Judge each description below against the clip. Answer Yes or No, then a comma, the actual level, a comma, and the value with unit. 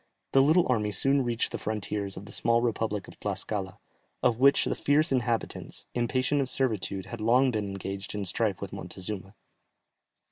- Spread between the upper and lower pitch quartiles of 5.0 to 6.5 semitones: No, average, 4.3 semitones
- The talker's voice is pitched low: Yes, low, 115 Hz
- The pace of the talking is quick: No, average, 170 wpm